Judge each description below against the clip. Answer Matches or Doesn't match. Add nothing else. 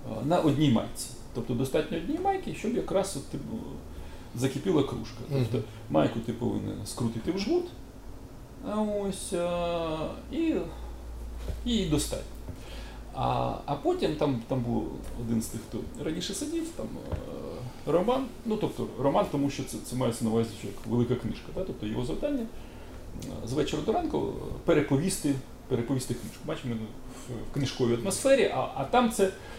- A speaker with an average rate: Matches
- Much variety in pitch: Matches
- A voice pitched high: Doesn't match